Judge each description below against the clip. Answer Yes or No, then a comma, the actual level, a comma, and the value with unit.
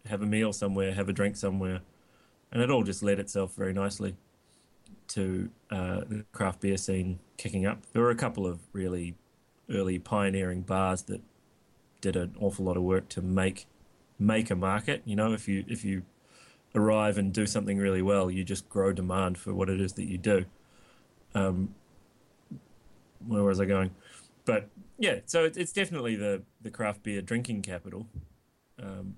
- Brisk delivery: No, average, 175 wpm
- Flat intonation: Yes, narrow, 2.0 semitones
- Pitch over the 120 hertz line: No, low, 100 Hz